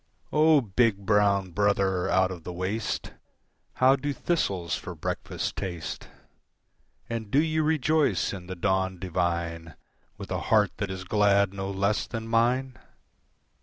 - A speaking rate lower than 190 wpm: Yes, average, 140 wpm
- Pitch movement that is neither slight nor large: Yes, average, 4.2 semitones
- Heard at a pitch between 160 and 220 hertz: No, low, 100 Hz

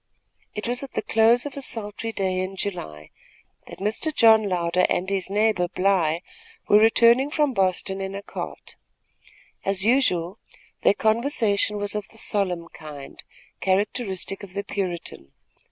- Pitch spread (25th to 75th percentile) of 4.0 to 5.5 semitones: No, average, 3.2 semitones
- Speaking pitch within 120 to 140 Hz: No, high, 200 Hz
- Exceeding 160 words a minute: No, average, 150 wpm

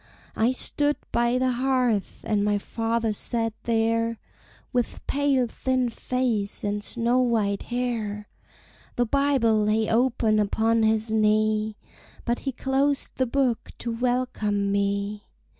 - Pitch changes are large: No, average, 2.8 semitones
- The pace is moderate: No, slow, 125 wpm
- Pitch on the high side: Yes, high, 230 Hz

